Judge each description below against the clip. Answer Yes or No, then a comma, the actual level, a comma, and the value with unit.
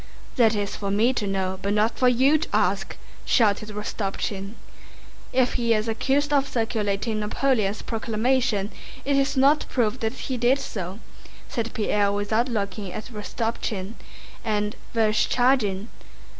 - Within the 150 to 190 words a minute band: No, average, 140 wpm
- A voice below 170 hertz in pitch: No, high, 220 Hz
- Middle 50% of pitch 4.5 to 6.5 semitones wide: No, average, 3.4 semitones